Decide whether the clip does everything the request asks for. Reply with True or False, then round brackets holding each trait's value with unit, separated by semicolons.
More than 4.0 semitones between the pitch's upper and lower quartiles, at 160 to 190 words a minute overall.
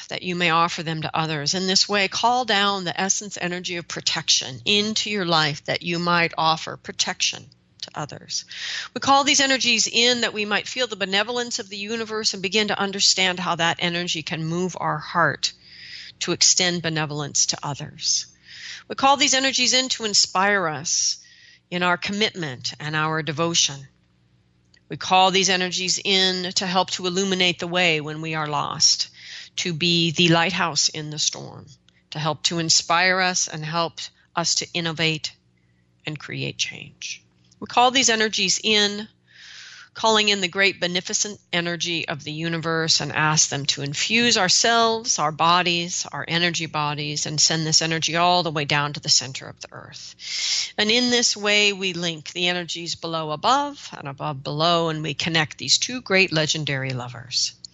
True (4.4 semitones; 175 wpm)